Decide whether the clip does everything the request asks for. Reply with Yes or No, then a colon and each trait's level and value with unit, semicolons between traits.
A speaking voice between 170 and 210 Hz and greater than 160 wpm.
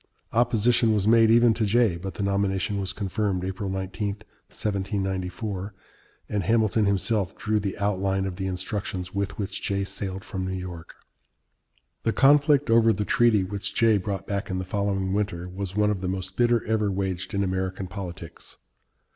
No: low, 100 Hz; average, 170 wpm